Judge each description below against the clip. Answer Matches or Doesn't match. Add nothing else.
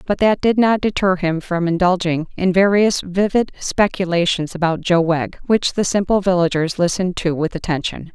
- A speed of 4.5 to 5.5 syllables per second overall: Matches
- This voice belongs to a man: Doesn't match